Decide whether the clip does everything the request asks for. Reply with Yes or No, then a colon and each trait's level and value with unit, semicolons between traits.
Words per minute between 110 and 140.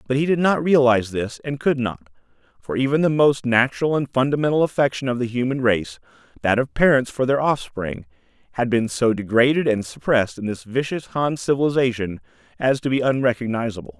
No: average, 180 wpm